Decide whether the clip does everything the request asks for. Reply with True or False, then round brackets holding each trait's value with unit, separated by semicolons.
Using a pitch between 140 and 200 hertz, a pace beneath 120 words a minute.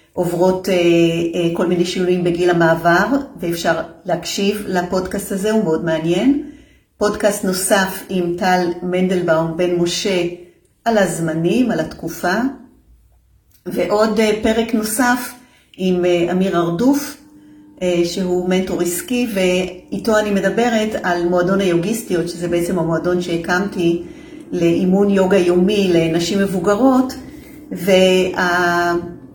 True (185 Hz; 110 wpm)